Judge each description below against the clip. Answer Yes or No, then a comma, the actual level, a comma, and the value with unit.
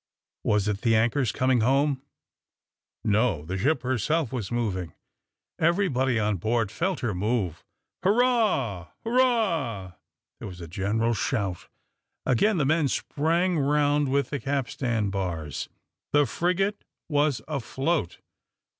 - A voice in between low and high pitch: No, low, 130 Hz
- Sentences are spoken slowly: Yes, slow, 120 wpm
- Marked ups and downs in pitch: Yes, wide, 6.6 semitones